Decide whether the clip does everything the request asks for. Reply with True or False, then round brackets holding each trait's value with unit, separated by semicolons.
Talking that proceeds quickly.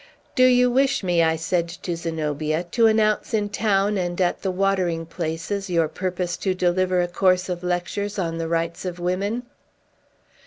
False (170 wpm)